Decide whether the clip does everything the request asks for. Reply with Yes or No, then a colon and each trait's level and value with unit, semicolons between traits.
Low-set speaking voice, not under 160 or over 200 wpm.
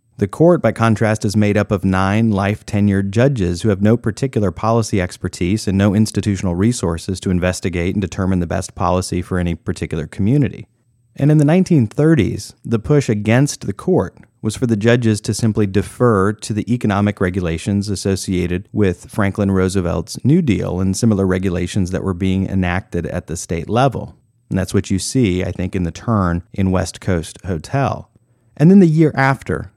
Yes: low, 100 Hz; average, 180 wpm